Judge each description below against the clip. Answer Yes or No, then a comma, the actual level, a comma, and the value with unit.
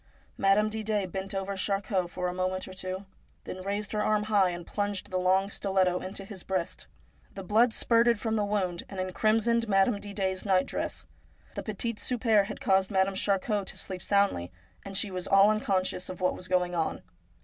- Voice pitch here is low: No, high, 195 Hz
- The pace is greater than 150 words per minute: Yes, average, 195 wpm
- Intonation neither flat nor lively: No, narrow, 2.1 semitones